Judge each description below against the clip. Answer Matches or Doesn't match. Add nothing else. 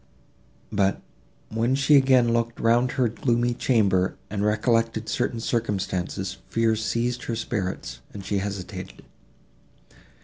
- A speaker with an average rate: Doesn't match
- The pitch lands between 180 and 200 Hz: Doesn't match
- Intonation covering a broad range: Doesn't match